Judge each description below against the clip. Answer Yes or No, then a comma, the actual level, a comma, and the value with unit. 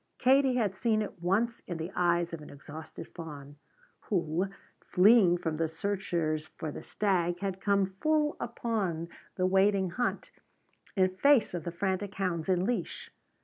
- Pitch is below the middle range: No, medium, 185 Hz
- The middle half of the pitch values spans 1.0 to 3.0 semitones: No, average, 3.6 semitones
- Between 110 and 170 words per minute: Yes, average, 155 wpm